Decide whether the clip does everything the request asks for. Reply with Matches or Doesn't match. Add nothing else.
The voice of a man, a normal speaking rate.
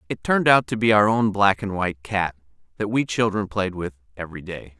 Doesn't match